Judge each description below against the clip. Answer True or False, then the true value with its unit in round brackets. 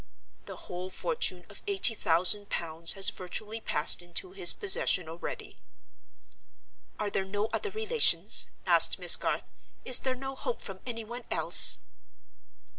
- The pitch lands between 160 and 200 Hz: False (215 Hz)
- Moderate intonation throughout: False (7.1 semitones)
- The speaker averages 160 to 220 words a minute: False (140 wpm)